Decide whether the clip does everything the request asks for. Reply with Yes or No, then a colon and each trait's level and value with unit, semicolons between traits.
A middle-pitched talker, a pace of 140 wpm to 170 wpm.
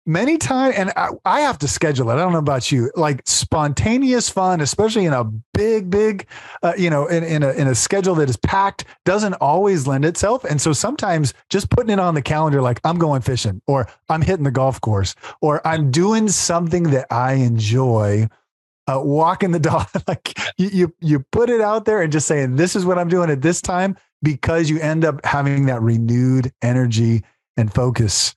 No: medium, 155 Hz; fast, 205 wpm